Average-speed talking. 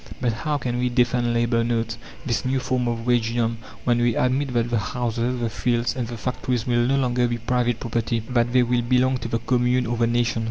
No: fast, 225 wpm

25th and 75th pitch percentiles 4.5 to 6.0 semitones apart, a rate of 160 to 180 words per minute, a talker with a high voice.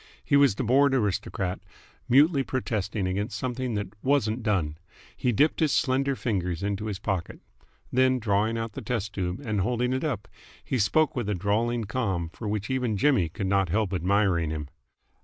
No: average, 4.8 semitones; average, 175 wpm; low, 110 Hz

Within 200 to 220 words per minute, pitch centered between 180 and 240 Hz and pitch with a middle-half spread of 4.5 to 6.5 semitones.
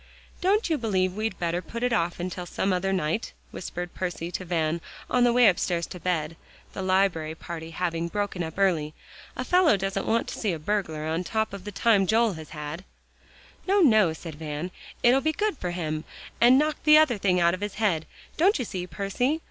Yes: fast, 205 wpm; medium, 185 Hz; average, 5.0 semitones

